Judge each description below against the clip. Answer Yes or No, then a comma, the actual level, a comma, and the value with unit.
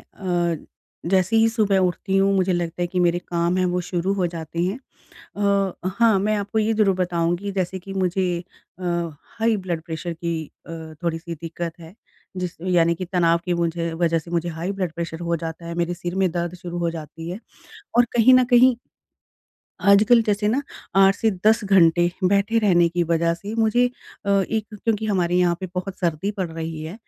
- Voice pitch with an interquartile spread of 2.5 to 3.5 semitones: Yes, average, 2.9 semitones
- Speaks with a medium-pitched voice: Yes, medium, 180 Hz